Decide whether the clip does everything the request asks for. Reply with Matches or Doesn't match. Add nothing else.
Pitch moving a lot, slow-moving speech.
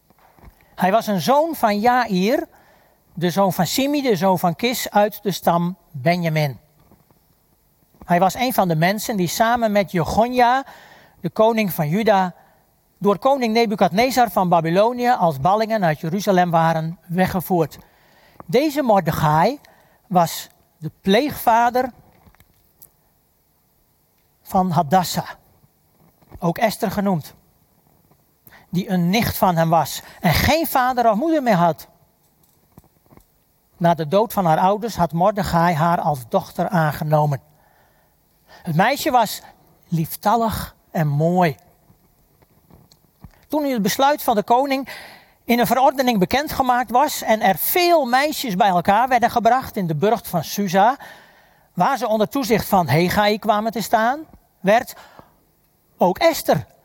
Matches